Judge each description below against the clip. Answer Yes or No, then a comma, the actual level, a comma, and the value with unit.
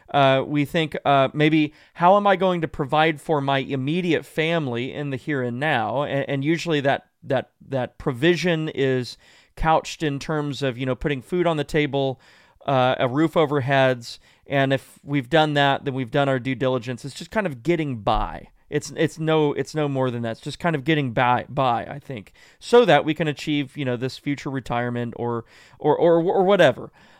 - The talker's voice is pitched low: No, medium, 145 Hz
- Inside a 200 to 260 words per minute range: Yes, fast, 205 wpm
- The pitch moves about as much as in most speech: Yes, average, 3.0 semitones